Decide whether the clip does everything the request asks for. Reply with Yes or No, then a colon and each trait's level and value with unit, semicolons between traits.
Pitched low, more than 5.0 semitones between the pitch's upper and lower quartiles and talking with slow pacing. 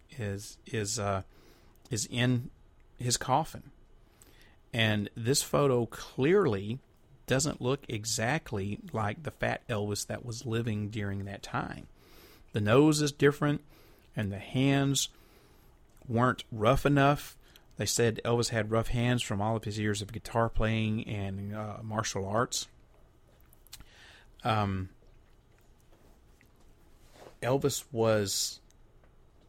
No: low, 115 Hz; average, 3.3 semitones; slow, 110 wpm